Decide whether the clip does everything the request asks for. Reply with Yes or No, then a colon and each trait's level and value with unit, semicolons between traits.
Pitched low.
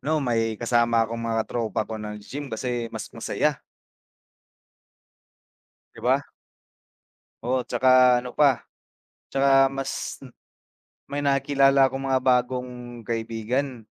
Yes: low, 125 Hz